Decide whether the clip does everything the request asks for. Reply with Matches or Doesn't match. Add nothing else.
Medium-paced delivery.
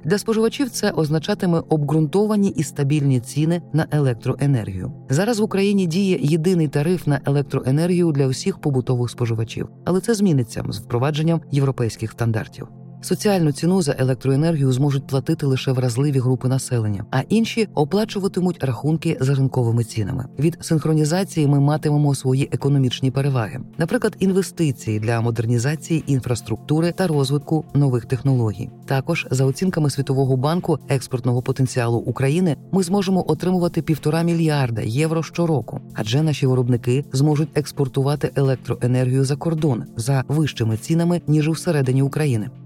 Matches